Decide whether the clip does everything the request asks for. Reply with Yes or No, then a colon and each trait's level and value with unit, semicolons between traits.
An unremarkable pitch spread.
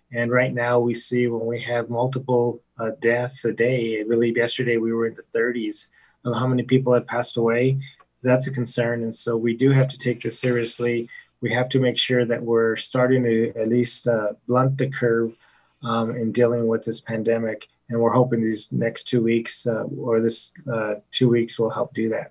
No: narrow, 1.3 semitones